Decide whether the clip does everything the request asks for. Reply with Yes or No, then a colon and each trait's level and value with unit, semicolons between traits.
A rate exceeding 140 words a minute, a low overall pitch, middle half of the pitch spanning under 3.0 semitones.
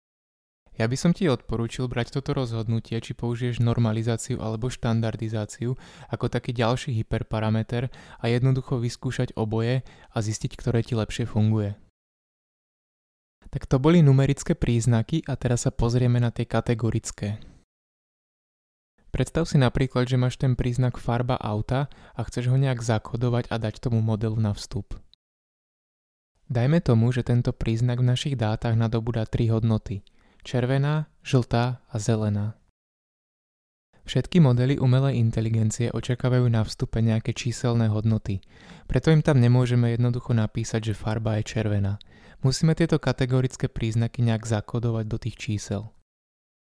No: average, 135 wpm; low, 120 Hz; narrow, 2.4 semitones